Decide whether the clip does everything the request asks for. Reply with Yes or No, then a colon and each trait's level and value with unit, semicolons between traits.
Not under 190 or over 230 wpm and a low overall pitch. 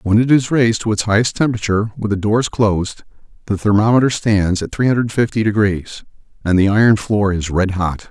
Yes: average, 200 wpm; low, 105 Hz